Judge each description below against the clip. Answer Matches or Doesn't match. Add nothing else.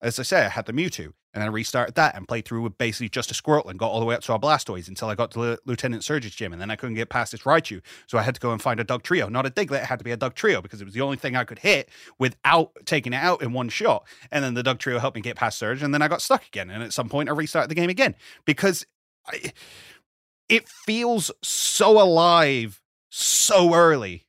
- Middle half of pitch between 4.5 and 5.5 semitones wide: Matches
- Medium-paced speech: Doesn't match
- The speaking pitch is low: Matches